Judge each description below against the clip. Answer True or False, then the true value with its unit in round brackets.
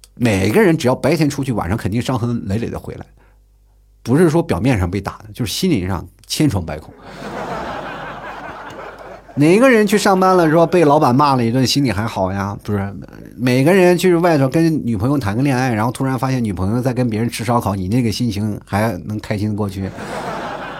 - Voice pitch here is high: False (120 Hz)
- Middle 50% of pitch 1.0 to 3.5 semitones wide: False (5.3 semitones)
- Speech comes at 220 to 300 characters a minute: True (295 characters per minute)